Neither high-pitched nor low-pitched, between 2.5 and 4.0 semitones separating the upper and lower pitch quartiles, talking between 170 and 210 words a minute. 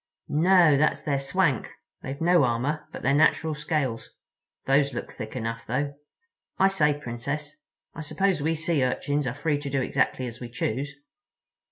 No: medium, 145 Hz; average, 3.3 semitones; average, 160 wpm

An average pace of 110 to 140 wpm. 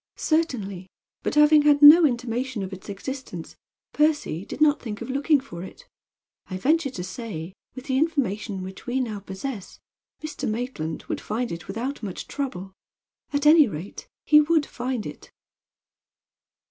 No: average, 155 wpm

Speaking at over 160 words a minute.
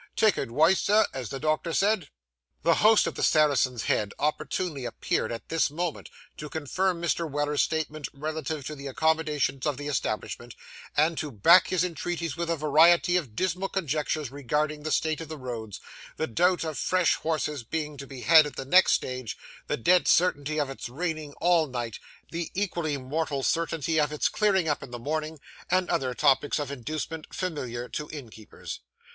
Yes: average, 180 wpm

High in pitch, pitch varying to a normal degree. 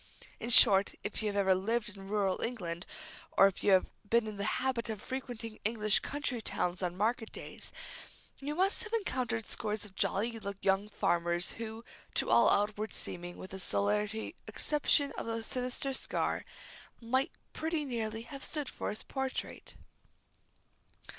Yes: high, 220 Hz; average, 3.9 semitones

